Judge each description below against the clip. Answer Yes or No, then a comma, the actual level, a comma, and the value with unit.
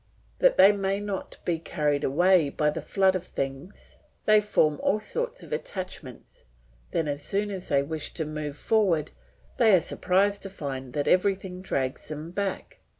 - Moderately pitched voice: Yes, medium, 180 Hz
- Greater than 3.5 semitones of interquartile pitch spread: Yes, average, 5.1 semitones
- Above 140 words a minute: Yes, average, 170 wpm